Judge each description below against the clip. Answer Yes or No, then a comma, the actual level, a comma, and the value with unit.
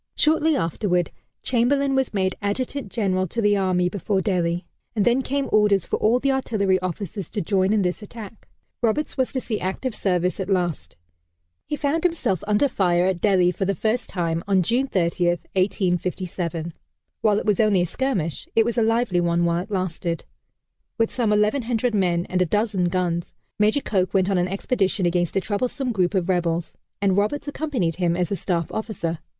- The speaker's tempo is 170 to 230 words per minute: Yes, average, 185 wpm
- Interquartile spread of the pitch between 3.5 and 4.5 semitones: Yes, average, 4.2 semitones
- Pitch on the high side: Yes, high, 195 Hz